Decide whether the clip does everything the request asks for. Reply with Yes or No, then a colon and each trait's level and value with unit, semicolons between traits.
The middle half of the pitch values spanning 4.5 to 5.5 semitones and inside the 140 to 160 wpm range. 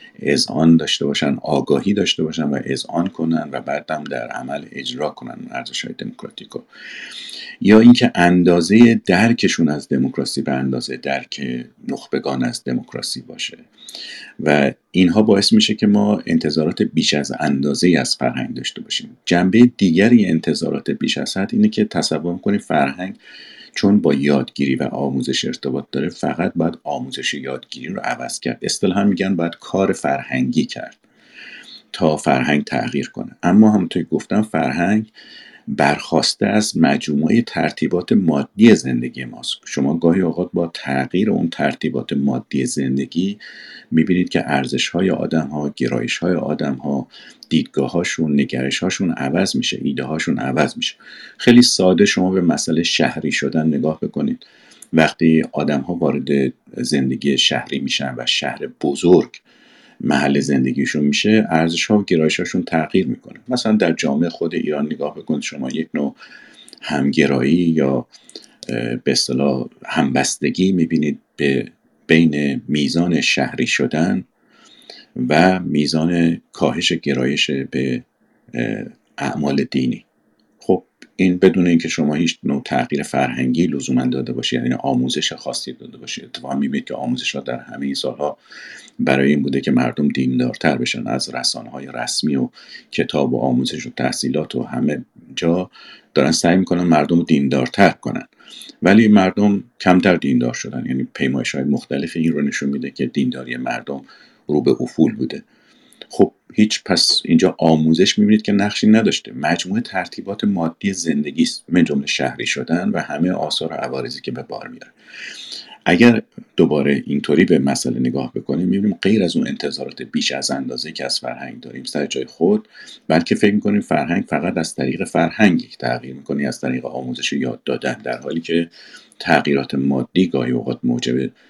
Yes: average, 5.2 semitones; average, 145 wpm